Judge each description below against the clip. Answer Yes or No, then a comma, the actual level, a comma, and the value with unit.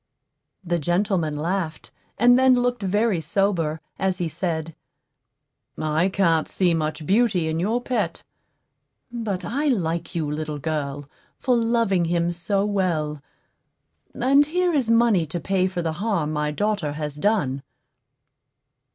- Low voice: No, medium, 180 Hz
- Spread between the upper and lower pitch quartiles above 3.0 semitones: Yes, wide, 5.4 semitones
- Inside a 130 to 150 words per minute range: Yes, average, 140 wpm